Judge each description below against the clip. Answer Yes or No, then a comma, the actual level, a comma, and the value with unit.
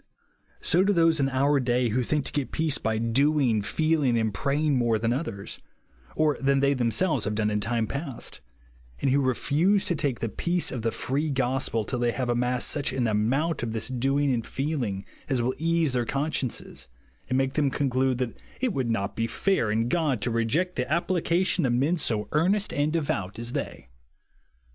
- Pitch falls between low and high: No, low, 130 Hz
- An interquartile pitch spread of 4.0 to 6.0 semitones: Yes, average, 4.5 semitones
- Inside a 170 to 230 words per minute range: Yes, average, 195 wpm